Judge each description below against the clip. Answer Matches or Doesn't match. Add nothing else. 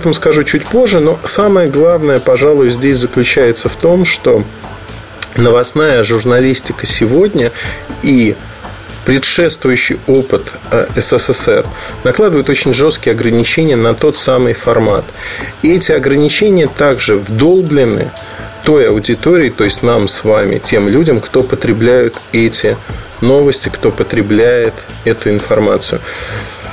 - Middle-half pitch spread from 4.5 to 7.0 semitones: Matches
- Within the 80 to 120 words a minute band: Matches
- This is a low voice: Matches